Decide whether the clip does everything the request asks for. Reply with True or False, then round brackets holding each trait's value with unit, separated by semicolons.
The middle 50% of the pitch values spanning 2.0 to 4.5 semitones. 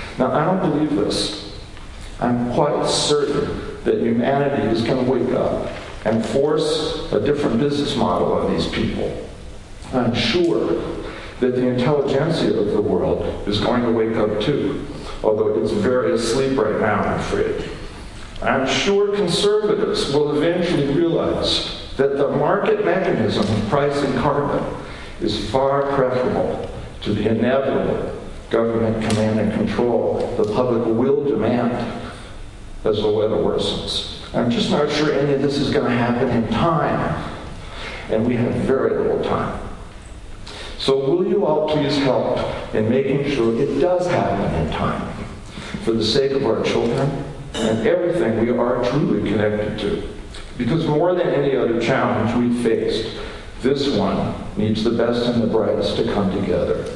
False (5.1 semitones)